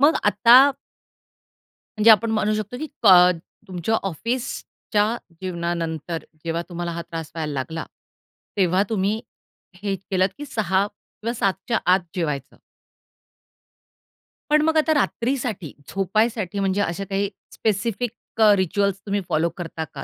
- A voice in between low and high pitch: No, high, 200 Hz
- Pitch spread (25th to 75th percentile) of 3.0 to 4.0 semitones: No, average, 4.5 semitones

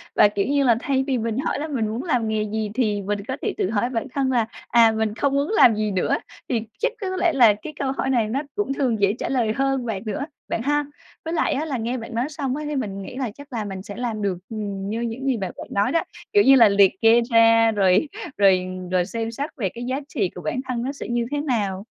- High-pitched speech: Yes, high, 230 Hz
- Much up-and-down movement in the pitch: No, average, 4.4 semitones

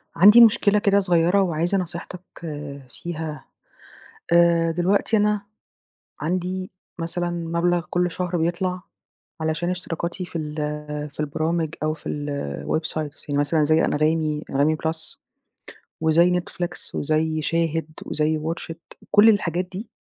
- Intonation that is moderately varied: No, narrow, 2.3 semitones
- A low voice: No, medium, 170 Hz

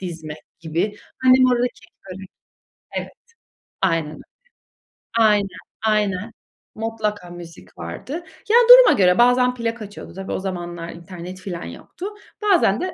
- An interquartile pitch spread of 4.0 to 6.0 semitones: Yes, average, 4.9 semitones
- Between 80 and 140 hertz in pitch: No, high, 195 Hz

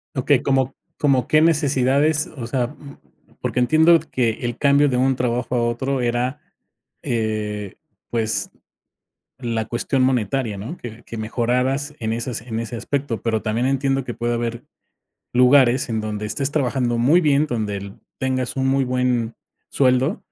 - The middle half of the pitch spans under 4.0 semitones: Yes, average, 2.7 semitones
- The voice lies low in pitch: Yes, low, 125 Hz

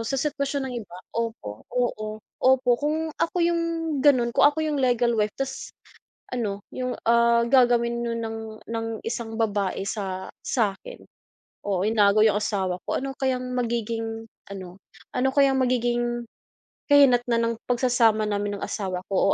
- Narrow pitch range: No, average, 3.2 semitones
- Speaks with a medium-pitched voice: No, high, 235 Hz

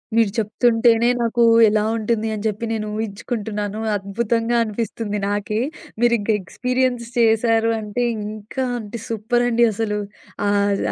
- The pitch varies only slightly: Yes, narrow, 2.1 semitones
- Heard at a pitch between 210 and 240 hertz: Yes, high, 225 Hz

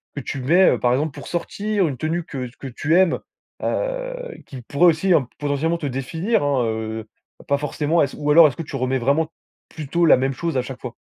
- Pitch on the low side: No, medium, 150 Hz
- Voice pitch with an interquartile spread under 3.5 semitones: No, average, 4.3 semitones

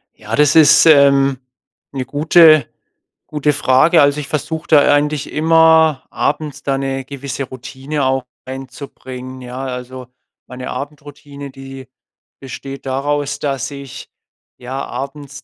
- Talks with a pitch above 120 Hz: Yes, medium, 140 Hz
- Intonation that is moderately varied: No, narrow, 2.0 semitones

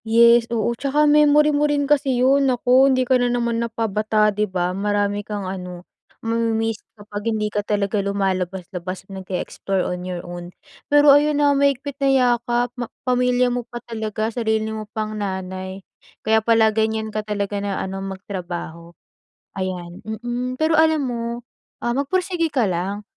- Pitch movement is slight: No, average, 4.2 semitones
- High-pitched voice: Yes, high, 220 Hz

